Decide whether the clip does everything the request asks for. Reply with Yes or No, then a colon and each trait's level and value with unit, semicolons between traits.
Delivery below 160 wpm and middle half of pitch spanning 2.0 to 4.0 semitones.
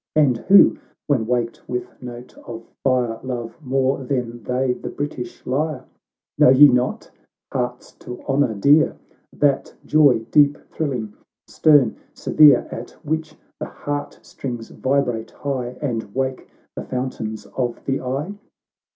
Yes: average, 140 wpm; average, 2.8 semitones